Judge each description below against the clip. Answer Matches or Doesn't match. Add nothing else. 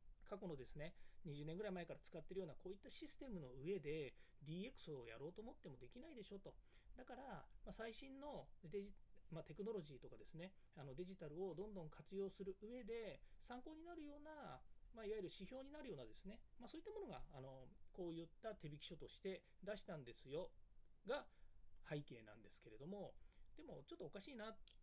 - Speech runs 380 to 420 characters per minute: Matches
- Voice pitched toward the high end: Matches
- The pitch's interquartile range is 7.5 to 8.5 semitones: Doesn't match